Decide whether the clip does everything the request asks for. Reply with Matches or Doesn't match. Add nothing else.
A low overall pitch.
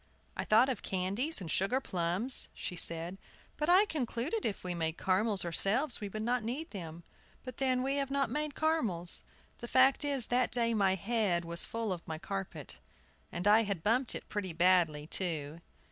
Doesn't match